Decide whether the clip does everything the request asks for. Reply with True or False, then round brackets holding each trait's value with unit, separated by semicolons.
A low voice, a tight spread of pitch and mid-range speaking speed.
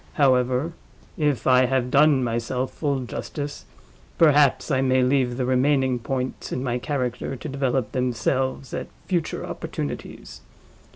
False (130 Hz; 2.0 semitones; 130 wpm)